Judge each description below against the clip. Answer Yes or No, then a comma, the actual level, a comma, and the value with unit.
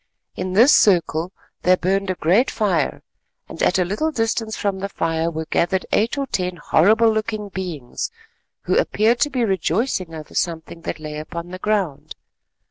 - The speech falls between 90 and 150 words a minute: No, average, 170 wpm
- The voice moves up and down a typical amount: Yes, average, 4.5 semitones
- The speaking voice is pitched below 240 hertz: Yes, medium, 185 Hz